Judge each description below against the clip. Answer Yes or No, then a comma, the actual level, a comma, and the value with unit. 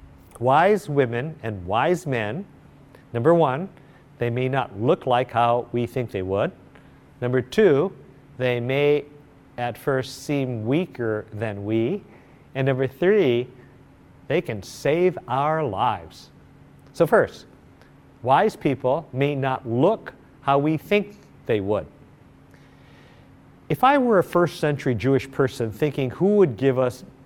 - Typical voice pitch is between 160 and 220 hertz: No, low, 135 Hz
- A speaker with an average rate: No, slow, 130 wpm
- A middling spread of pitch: Yes, average, 3.3 semitones